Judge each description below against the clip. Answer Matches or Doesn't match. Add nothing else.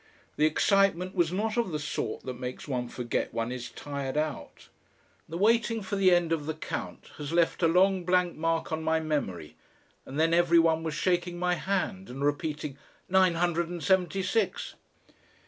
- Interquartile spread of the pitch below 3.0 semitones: Doesn't match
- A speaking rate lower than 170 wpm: Doesn't match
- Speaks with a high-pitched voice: Doesn't match